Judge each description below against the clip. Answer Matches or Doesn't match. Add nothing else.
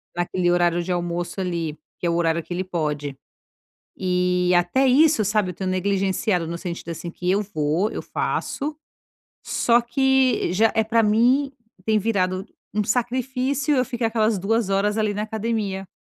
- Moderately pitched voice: Doesn't match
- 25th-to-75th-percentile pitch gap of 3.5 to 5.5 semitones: Matches